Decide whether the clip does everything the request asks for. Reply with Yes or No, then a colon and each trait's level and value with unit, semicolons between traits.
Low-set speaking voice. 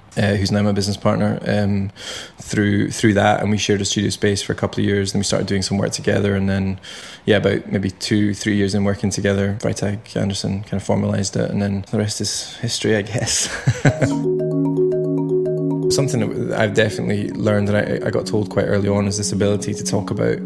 Yes: low, 100 Hz